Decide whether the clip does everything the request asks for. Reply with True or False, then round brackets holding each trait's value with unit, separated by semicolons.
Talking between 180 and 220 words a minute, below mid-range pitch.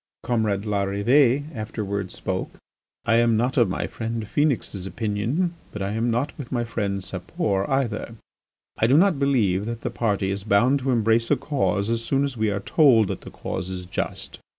True (185 wpm; 115 Hz)